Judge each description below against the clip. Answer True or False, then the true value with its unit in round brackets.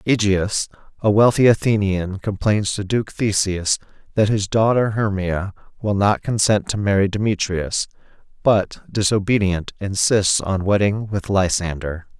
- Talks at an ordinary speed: False (125 wpm)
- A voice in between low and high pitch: False (100 Hz)